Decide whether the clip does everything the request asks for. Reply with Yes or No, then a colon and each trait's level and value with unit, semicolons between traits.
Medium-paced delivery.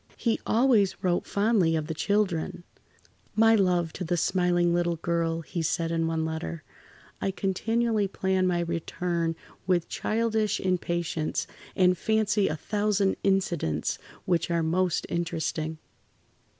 No: slow, 130 wpm